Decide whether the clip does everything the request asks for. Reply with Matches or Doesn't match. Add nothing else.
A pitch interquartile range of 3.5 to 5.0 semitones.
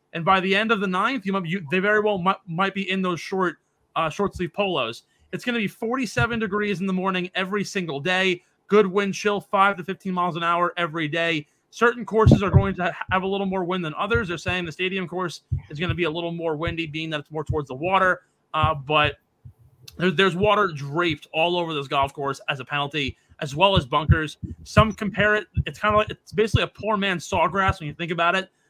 Matches